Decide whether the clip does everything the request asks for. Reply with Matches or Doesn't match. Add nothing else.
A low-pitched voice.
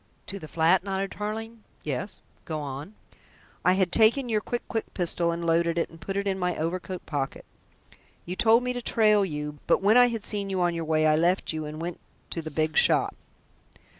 Doesn't match